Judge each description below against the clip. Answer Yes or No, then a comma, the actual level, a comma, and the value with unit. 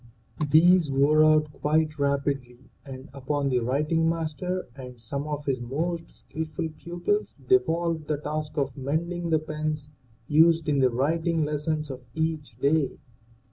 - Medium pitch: Yes, medium, 150 Hz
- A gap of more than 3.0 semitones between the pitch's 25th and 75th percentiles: No, narrow, 2.6 semitones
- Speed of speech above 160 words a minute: No, average, 140 wpm